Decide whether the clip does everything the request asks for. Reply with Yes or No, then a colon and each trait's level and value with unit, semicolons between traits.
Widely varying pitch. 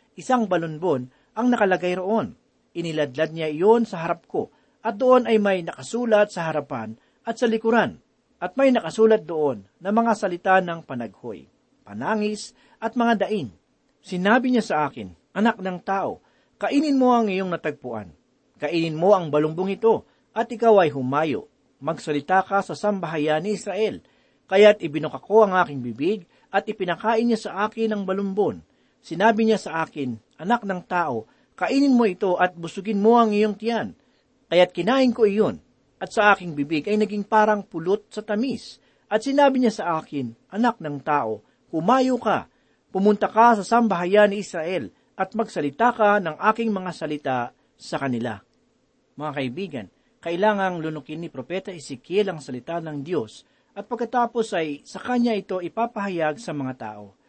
Yes: wide, 5.9 semitones